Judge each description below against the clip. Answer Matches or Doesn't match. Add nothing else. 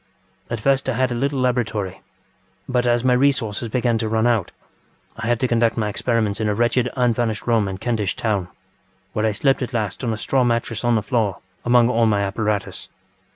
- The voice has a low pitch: Matches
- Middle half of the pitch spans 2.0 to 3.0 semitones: Matches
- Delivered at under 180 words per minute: Doesn't match